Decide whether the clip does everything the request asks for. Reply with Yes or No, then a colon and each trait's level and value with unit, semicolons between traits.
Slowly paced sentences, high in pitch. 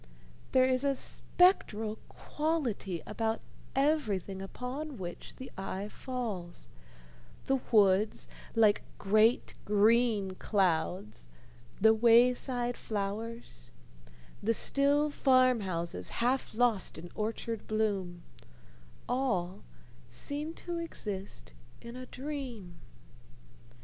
Yes: slow, 95 wpm; high, 225 Hz